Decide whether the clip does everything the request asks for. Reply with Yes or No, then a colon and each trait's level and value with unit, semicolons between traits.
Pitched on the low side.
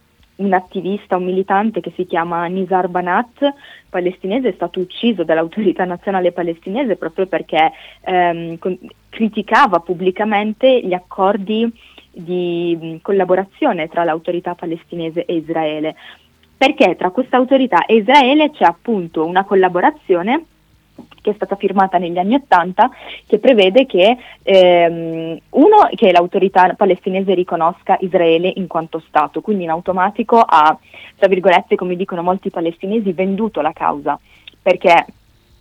No: medium, 185 Hz